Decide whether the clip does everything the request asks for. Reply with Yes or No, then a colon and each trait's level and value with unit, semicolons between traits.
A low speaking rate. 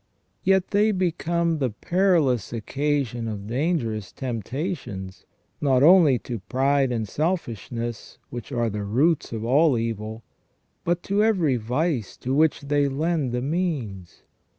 Yes: slow, 130 wpm